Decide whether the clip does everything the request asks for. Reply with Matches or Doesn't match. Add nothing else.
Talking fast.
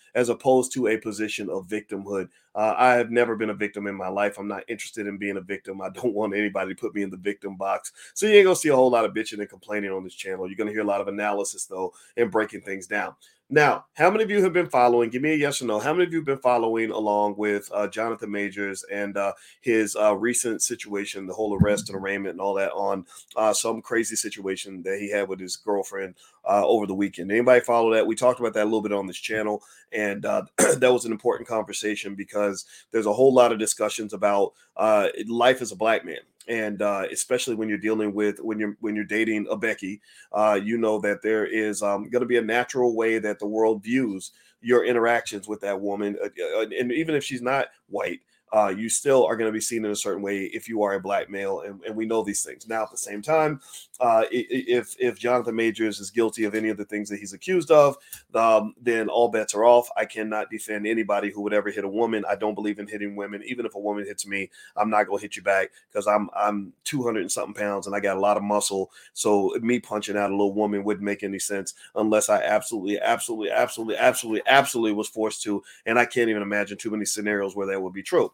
Matches